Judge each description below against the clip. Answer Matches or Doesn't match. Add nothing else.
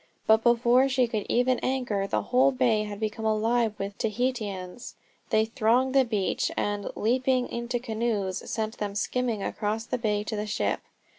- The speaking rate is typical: Matches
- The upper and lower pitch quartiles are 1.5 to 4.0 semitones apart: Matches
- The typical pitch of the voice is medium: Doesn't match